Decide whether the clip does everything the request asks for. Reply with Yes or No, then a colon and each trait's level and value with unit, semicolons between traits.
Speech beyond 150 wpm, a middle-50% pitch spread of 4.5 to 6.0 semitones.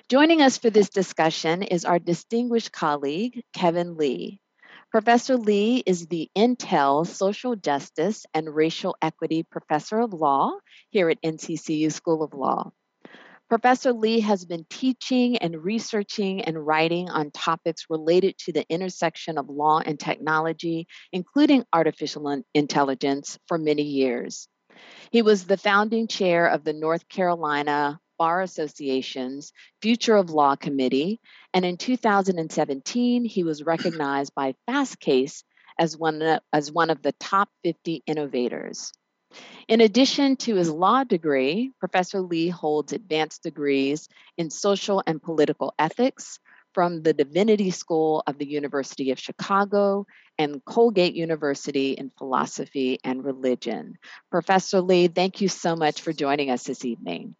No: slow, 135 wpm; average, 5.1 semitones